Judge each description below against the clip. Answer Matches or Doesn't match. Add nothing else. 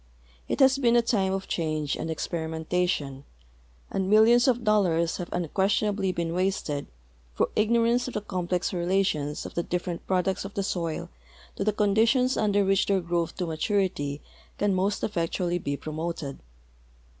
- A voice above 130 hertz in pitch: Matches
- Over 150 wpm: Matches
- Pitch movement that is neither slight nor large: Matches